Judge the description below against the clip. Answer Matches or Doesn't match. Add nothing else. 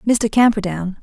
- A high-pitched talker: Matches